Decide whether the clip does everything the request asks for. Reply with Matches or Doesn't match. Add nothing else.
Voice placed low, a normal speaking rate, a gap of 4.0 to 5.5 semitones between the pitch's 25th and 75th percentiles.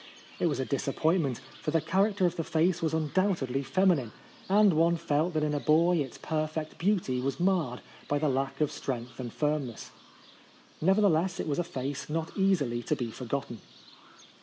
Doesn't match